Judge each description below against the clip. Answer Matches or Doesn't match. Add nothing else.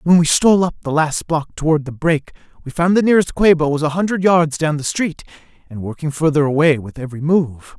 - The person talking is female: Doesn't match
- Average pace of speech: Doesn't match